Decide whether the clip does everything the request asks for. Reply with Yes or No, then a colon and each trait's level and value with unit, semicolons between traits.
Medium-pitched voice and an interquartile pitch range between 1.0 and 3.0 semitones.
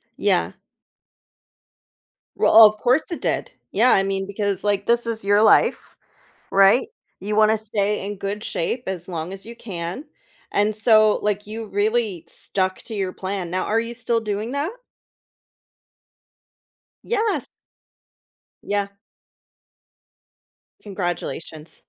No: high, 205 Hz; narrow, 2.6 semitones